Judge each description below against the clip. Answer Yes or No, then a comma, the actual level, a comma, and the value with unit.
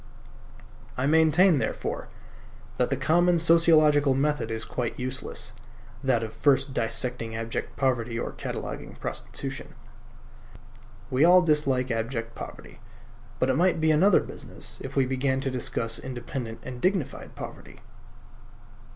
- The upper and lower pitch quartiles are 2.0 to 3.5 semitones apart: No, average, 4.3 semitones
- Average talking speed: No, slow, 125 wpm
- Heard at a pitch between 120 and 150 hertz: Yes, low, 135 Hz